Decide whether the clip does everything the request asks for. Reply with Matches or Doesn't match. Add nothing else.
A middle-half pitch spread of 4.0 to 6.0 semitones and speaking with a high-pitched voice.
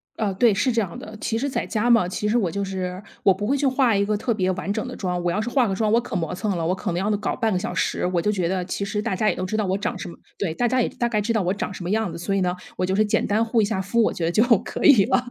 Doesn't match